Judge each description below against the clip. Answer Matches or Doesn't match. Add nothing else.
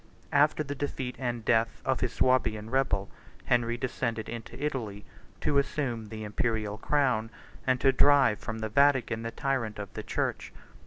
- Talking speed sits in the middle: Matches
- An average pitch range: Matches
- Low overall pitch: Matches